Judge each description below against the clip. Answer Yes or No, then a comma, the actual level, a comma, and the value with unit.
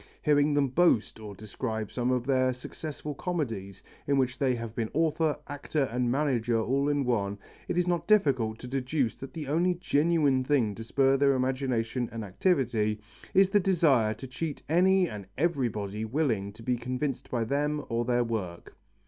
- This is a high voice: No, low, 130 Hz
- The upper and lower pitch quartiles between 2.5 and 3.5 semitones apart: No, average, 4.6 semitones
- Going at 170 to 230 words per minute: Yes, average, 175 wpm